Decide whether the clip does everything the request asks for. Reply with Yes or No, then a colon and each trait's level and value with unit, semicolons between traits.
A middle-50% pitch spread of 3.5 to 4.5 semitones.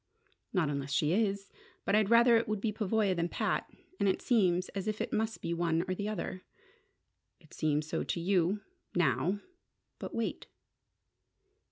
Yes: average, 4.0 semitones